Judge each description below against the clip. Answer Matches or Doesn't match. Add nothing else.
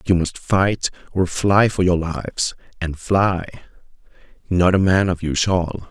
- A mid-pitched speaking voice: Doesn't match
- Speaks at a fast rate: Doesn't match